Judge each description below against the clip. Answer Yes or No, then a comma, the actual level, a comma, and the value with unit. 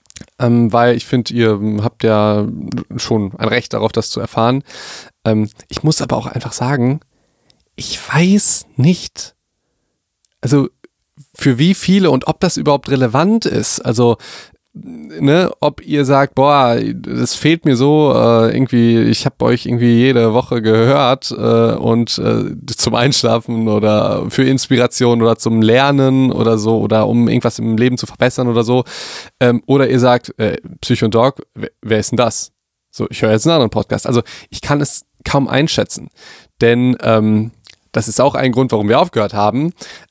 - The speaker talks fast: No, average, 170 wpm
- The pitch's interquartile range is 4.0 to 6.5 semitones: No, average, 3.1 semitones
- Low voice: Yes, low, 120 Hz